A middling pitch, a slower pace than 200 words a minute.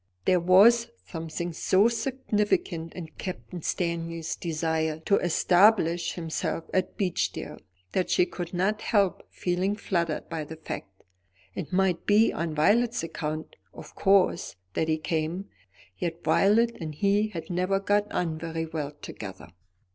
Yes: medium, 175 Hz; average, 140 wpm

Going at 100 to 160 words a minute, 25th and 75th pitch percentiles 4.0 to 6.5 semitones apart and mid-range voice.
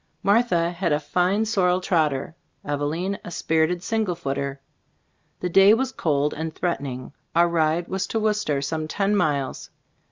Yes: average, 155 wpm; average, 4.5 semitones; medium, 170 Hz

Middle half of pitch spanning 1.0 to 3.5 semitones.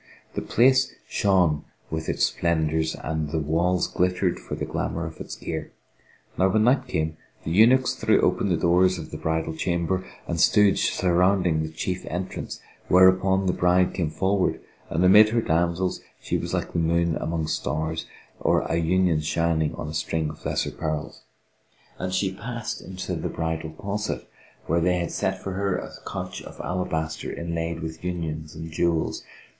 Yes: average, 2.7 semitones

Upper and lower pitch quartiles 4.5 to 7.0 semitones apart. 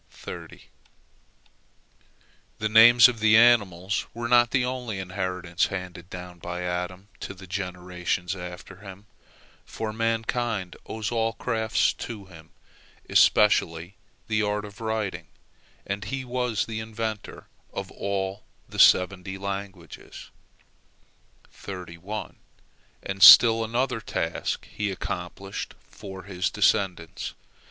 No: average, 3.4 semitones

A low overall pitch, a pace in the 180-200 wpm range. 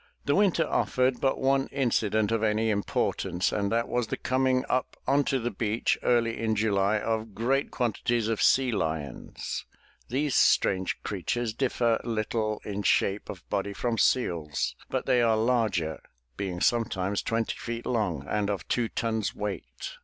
No: low, 115 Hz; average, 155 wpm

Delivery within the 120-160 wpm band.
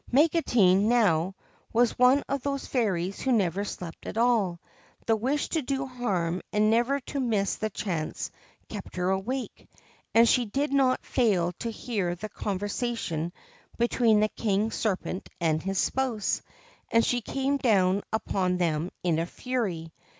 Yes: average, 150 wpm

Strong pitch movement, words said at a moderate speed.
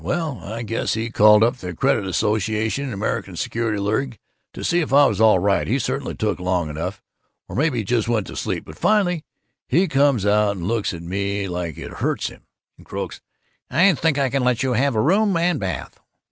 No: wide, 5.8 semitones; fast, 215 wpm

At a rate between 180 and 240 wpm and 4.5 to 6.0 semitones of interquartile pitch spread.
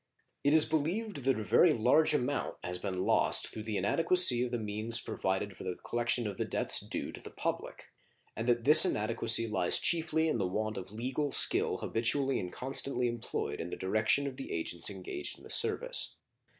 Yes: average, 190 wpm; wide, 5.4 semitones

